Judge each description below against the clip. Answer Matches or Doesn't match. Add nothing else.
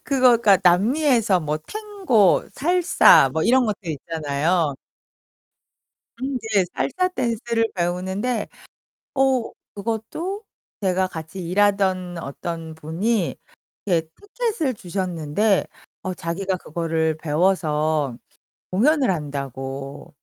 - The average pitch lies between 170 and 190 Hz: Matches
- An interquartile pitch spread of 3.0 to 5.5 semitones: Doesn't match